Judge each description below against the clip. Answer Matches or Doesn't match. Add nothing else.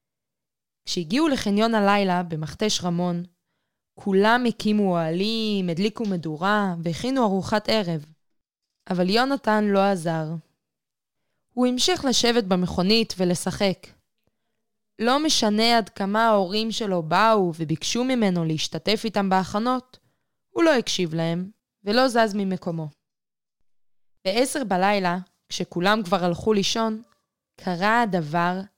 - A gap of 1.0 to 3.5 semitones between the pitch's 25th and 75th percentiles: Doesn't match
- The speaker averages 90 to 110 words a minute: Matches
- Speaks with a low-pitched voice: Doesn't match